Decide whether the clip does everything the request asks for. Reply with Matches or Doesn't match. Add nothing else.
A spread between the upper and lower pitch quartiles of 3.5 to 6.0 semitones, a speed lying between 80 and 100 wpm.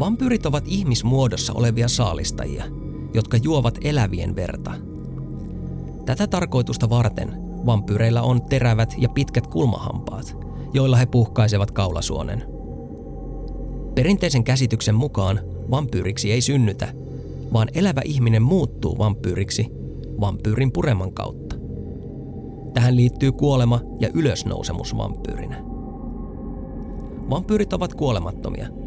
Matches